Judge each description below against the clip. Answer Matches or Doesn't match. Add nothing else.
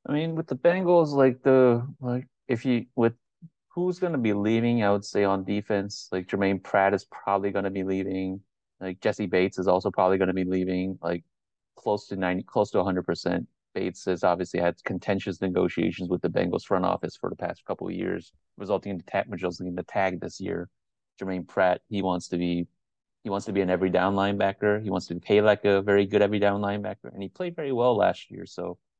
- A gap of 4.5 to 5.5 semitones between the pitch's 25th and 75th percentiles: Doesn't match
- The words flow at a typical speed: Doesn't match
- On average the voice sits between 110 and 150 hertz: Doesn't match